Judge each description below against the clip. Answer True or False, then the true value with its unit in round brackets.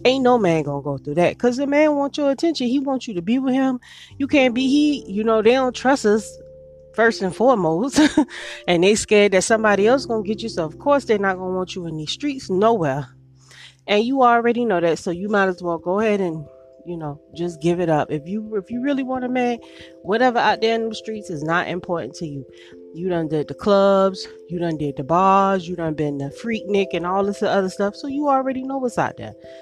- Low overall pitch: False (200 Hz)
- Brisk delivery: True (245 wpm)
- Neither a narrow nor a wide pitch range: False (6.7 semitones)